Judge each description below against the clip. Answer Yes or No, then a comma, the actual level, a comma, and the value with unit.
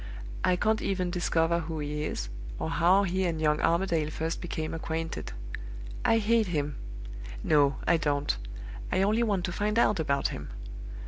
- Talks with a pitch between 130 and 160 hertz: No, medium, 170 Hz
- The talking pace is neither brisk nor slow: Yes, average, 165 wpm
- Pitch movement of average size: Yes, average, 3.7 semitones